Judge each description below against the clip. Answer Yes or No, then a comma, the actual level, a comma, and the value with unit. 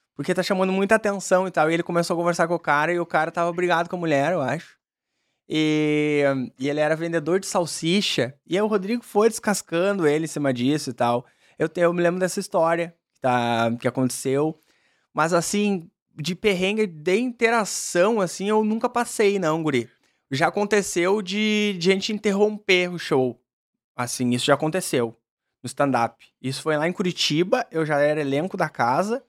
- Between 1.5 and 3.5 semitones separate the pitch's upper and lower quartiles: No, average, 5.1 semitones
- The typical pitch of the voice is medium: Yes, medium, 170 Hz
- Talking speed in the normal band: No, fast, 190 wpm